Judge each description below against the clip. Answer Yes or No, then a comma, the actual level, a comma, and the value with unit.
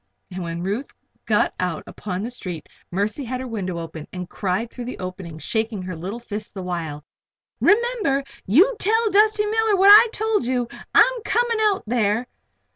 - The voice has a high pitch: Yes, high, 230 Hz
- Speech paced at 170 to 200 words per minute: Yes, average, 175 wpm